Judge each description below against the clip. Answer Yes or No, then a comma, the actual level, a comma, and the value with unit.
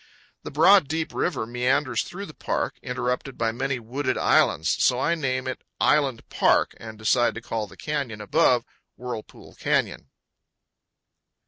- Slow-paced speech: No, average, 145 wpm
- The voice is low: Yes, low, 130 Hz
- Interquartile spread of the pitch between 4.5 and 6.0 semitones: No, average, 3.9 semitones